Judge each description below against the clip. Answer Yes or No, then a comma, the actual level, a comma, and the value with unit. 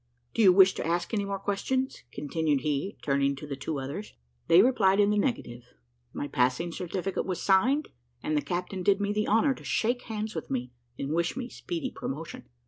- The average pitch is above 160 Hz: Yes, medium, 185 Hz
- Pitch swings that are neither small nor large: No, wide, 6.3 semitones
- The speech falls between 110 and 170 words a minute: No, average, 200 wpm